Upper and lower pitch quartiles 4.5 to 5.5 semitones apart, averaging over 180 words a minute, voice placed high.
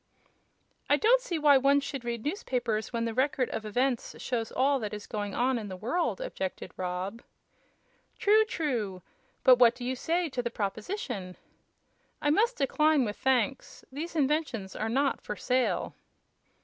No: average, 5.1 semitones; average, 160 wpm; very high, 255 Hz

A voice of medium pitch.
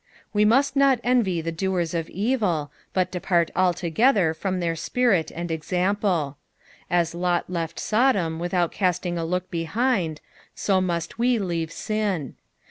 Yes: medium, 180 Hz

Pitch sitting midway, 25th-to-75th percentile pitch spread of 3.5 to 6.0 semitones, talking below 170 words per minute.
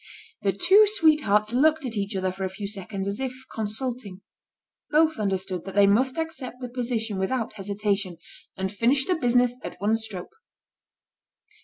No: high, 220 Hz; average, 4.7 semitones; average, 160 wpm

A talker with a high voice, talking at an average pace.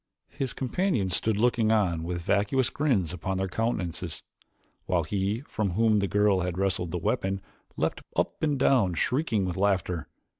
No: low, 100 Hz; average, 160 wpm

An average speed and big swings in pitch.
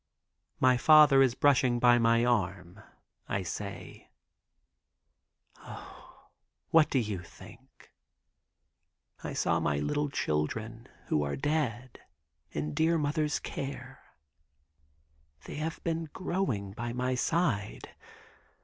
No: slow, 105 wpm; wide, 6.2 semitones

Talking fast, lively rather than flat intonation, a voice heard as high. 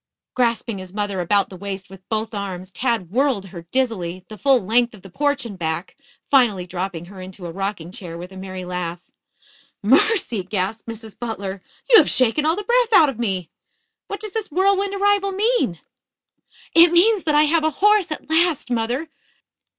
No: average, 185 wpm; wide, 8.7 semitones; high, 225 Hz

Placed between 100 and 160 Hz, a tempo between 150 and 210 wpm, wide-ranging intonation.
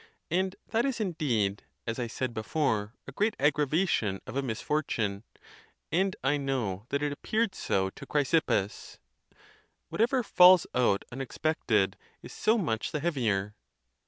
No: medium, 140 Hz; slow, 135 wpm; wide, 7.9 semitones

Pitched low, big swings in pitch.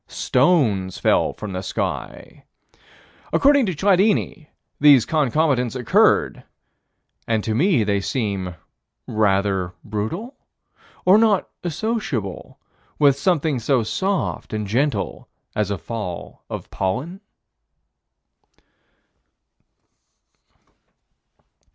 Yes: low, 125 Hz; wide, 8.9 semitones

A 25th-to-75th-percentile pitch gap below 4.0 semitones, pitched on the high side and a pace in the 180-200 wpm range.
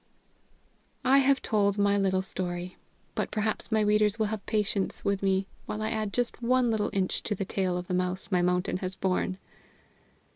Yes: narrow, 2.6 semitones; high, 200 Hz; average, 185 wpm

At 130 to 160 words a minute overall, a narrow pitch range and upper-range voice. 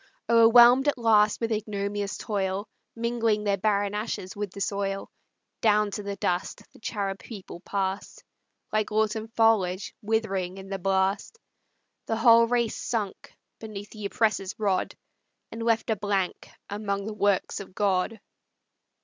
Yes: average, 140 wpm; narrow, 2.2 semitones; high, 210 Hz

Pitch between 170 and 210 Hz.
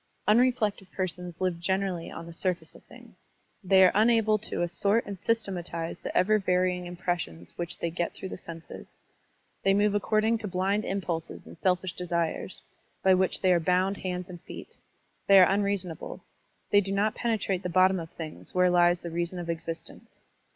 Yes: medium, 185 Hz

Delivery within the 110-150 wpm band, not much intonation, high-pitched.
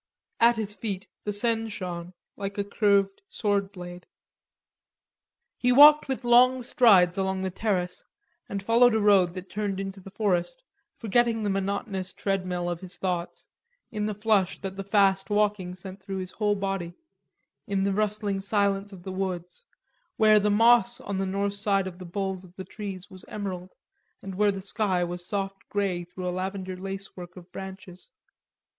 No: average, 175 wpm; narrow, 2.1 semitones; high, 195 Hz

